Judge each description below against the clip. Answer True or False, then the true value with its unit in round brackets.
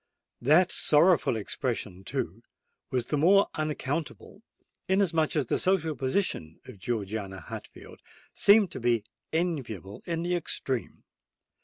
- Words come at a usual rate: False (120 wpm)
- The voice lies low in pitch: False (145 Hz)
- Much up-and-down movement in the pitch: True (7.1 semitones)